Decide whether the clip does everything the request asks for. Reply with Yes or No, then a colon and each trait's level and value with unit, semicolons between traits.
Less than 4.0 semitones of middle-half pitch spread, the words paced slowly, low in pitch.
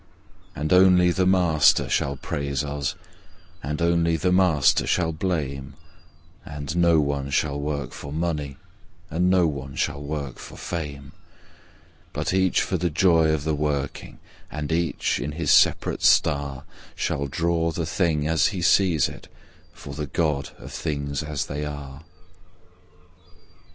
No: average, 3.0 semitones; average, 145 wpm; very low, 75 Hz